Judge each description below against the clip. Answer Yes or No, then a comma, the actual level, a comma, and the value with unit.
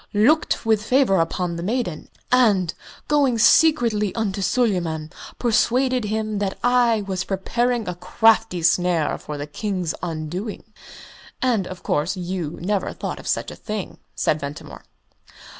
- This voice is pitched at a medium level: No, high, 200 Hz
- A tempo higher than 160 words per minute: No, average, 140 wpm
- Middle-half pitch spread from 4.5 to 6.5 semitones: Yes, average, 4.9 semitones